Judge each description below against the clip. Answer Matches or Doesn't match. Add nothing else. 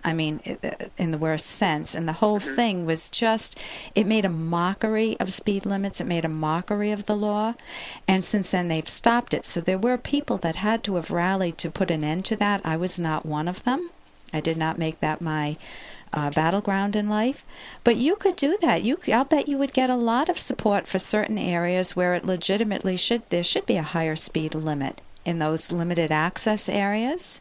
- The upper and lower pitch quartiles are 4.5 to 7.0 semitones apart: Matches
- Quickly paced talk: Matches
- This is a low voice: Doesn't match